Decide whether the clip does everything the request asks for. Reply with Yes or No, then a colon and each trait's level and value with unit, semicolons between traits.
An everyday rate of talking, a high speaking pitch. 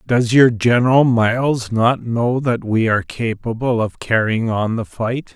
No: average, 170 wpm; low, 115 Hz